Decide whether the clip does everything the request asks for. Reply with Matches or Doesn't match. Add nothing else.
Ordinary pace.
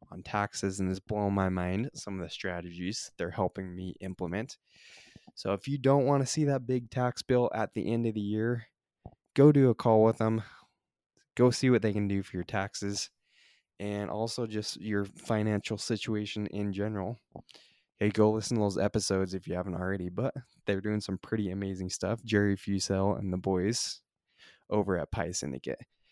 Matches